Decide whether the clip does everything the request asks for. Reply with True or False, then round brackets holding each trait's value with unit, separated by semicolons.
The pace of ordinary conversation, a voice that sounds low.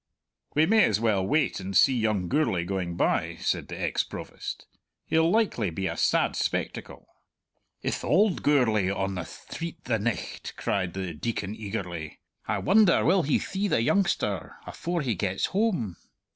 True (160 wpm; 110 Hz)